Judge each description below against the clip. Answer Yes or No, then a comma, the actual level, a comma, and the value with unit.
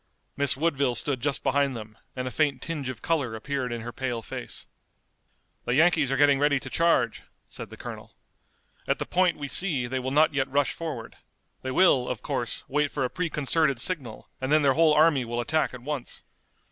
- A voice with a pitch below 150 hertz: Yes, medium, 140 Hz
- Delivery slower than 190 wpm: No, average, 200 wpm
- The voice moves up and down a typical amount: Yes, average, 3.2 semitones